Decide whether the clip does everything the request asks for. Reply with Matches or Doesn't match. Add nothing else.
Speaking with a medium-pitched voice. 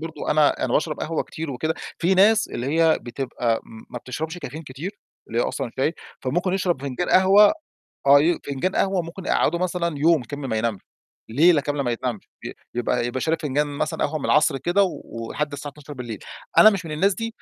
Matches